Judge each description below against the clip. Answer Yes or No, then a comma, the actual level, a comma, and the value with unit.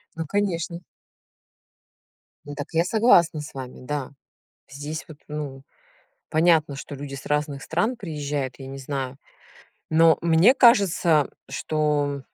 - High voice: No, medium, 150 Hz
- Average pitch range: Yes, average, 3.0 semitones